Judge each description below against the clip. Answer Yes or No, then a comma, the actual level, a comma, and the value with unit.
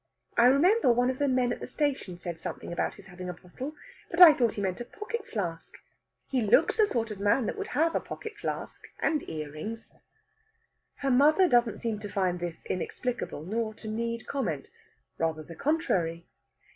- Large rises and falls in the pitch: Yes, wide, 7.6 semitones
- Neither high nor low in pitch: No, high, 230 Hz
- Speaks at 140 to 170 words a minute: No, average, 190 wpm